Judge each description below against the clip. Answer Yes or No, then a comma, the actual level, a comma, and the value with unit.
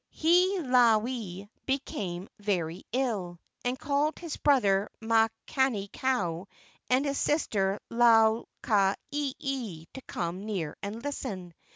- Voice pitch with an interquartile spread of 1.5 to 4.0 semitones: No, wide, 5.5 semitones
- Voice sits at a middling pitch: No, high, 225 Hz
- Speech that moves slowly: Yes, slow, 105 wpm